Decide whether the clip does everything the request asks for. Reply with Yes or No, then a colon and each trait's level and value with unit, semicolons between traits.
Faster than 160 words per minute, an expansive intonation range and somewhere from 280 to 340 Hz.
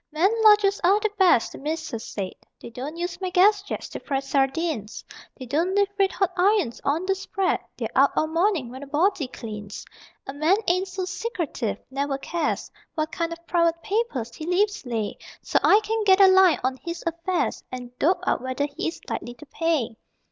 Yes: average, 200 wpm; wide, 5.9 semitones; very high, 335 Hz